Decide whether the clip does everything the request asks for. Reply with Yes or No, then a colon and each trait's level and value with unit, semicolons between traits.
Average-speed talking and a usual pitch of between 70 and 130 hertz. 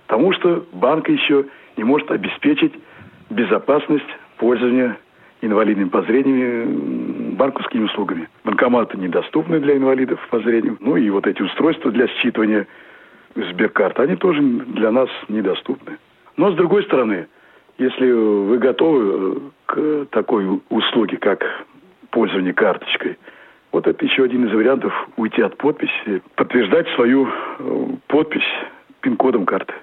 No: average, 120 wpm; medium, 140 Hz